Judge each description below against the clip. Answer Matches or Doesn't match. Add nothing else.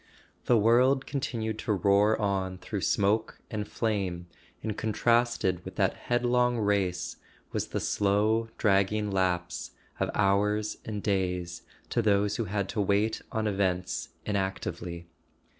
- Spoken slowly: Matches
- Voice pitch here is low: Matches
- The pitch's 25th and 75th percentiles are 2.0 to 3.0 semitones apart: Matches